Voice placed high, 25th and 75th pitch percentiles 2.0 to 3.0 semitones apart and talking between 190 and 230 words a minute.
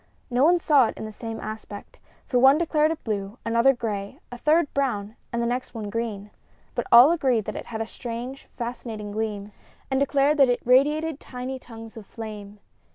No: high, 235 Hz; average, 3.8 semitones; average, 195 wpm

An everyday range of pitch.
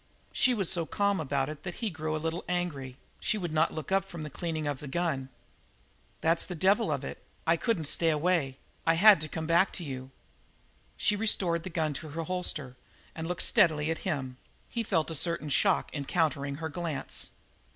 Yes: average, 3.1 semitones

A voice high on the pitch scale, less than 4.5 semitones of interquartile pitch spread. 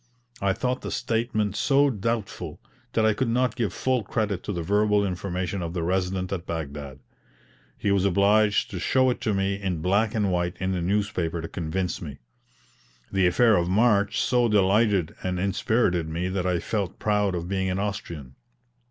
No: very low, 95 Hz; average, 3.1 semitones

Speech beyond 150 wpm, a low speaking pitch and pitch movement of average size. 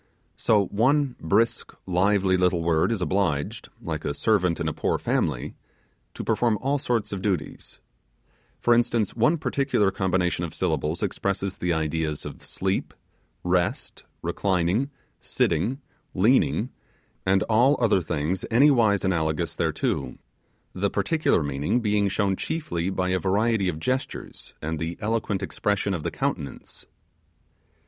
No: slow, 135 wpm; very low, 95 Hz; average, 4.7 semitones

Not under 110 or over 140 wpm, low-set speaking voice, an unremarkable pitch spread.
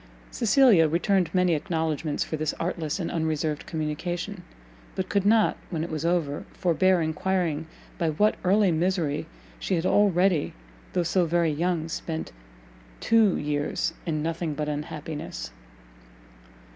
No: slow, 135 wpm; medium, 165 Hz; average, 3.0 semitones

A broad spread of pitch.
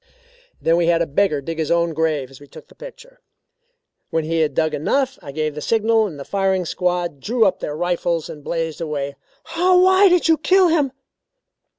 Yes: wide, 8.1 semitones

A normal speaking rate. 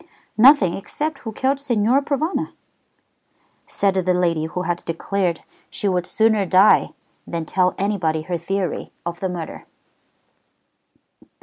No: slow, 125 wpm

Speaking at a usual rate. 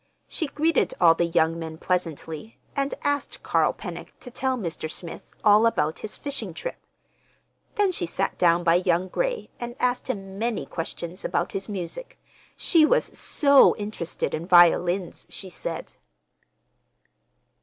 Yes: average, 145 wpm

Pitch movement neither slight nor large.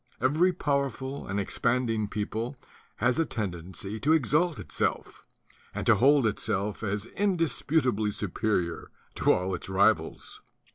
No: wide, 5.7 semitones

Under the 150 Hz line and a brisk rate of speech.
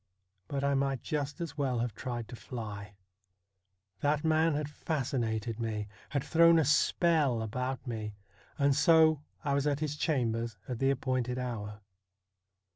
No: low, 135 Hz; average, 150 wpm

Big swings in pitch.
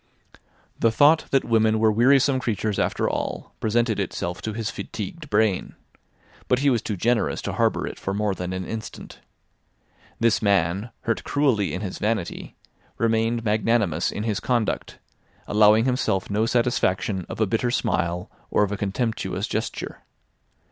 No: average, 2.7 semitones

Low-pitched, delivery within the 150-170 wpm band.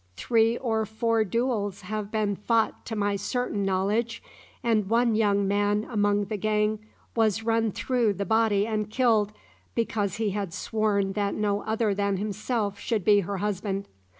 No: high, 210 Hz; average, 160 wpm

